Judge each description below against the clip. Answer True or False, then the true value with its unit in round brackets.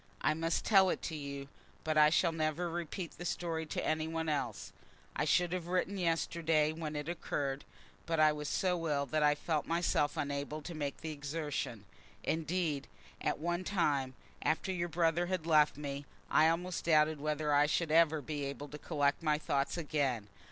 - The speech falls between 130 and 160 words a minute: False (185 wpm)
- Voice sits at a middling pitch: True (155 Hz)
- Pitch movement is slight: True (2.3 semitones)